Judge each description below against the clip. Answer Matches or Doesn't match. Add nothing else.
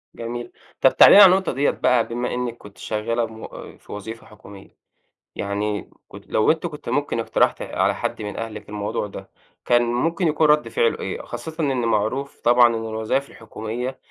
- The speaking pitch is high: Doesn't match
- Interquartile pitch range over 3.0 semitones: Matches